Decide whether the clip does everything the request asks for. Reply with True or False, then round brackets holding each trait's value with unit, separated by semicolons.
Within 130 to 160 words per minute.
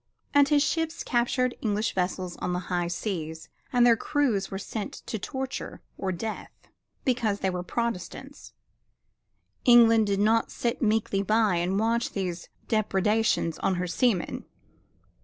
True (140 wpm)